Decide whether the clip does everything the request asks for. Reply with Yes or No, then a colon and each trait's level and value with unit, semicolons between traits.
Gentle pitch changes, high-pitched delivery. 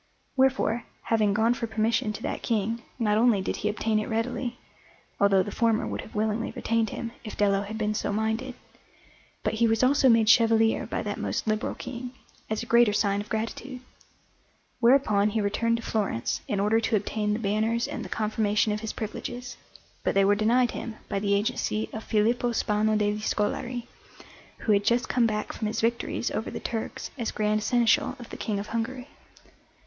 Yes: narrow, 1.9 semitones; high, 220 Hz